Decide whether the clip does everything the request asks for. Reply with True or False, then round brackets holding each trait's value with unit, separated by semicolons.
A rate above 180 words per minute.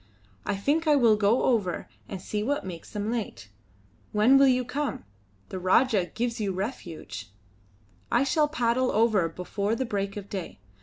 False (165 wpm)